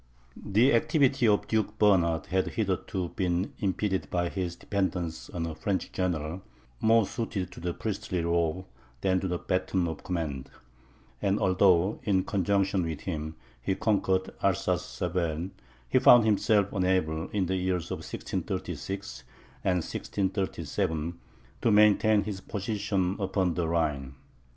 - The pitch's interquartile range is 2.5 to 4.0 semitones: Yes, average, 2.9 semitones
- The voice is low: Yes, very low, 95 Hz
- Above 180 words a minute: No, slow, 135 wpm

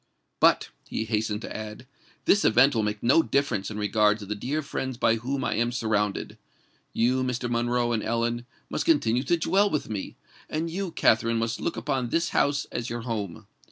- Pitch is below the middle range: Yes, low, 120 Hz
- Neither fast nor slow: Yes, average, 195 wpm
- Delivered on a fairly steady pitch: No, average, 3.4 semitones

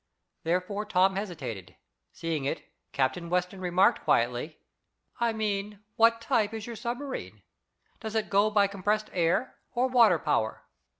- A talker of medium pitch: No, high, 200 Hz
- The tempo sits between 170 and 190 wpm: No, slow, 135 wpm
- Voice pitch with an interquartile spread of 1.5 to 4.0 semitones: No, average, 4.4 semitones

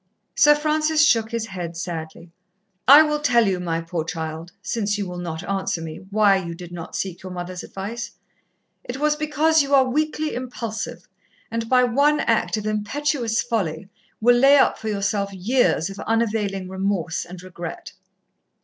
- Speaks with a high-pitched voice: Yes, high, 210 Hz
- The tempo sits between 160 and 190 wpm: Yes, average, 165 wpm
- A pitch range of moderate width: No, wide, 6.1 semitones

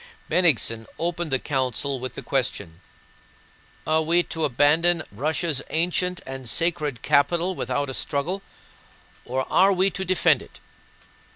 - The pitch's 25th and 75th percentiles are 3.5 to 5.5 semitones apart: Yes, average, 4.8 semitones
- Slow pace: Yes, slow, 130 wpm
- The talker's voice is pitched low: No, medium, 155 Hz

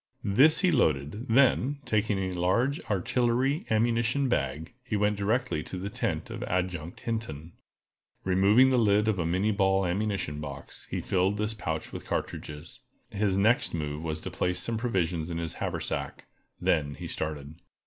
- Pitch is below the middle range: Yes, low, 100 Hz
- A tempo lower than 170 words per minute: Yes, average, 160 wpm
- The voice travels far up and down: Yes, wide, 5.7 semitones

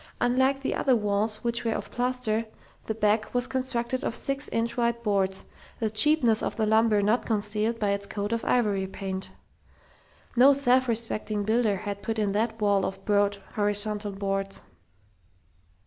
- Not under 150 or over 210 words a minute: Yes, average, 165 wpm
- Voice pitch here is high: Yes, high, 220 Hz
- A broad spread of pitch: No, average, 2.7 semitones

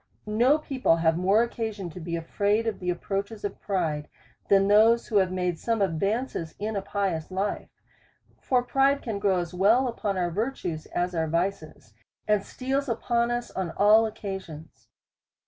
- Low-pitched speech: No, high, 200 Hz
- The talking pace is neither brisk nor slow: Yes, average, 165 wpm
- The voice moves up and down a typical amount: Yes, average, 4.4 semitones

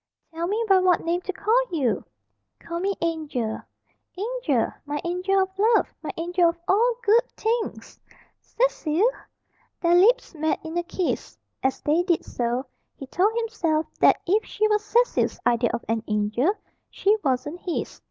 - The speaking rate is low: No, average, 160 wpm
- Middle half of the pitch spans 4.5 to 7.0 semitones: Yes, wide, 5.6 semitones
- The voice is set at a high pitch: Yes, very high, 350 Hz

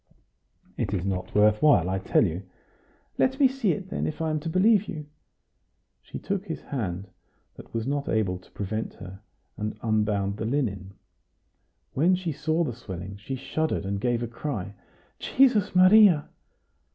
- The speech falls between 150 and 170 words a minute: Yes, average, 165 wpm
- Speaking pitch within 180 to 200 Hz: No, low, 120 Hz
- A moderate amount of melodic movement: No, wide, 8.8 semitones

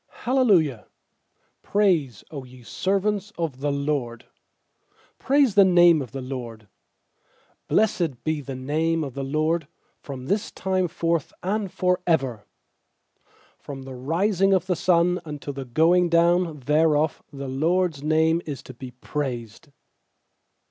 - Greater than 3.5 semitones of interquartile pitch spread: Yes, average, 5.0 semitones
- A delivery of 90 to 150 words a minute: Yes, average, 140 wpm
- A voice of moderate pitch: Yes, medium, 155 Hz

